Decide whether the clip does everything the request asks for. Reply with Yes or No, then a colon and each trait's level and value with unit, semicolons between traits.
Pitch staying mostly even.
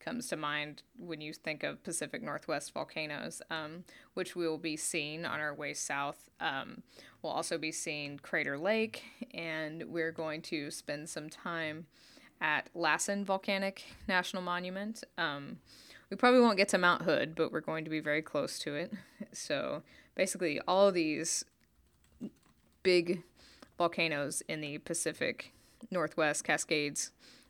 No: average, 3.3 semitones